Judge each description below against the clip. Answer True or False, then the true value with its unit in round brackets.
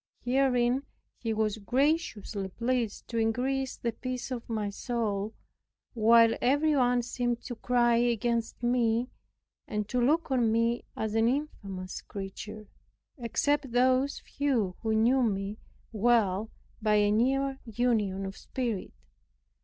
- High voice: True (235 Hz)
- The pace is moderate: False (130 wpm)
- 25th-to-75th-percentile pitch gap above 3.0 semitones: False (2.7 semitones)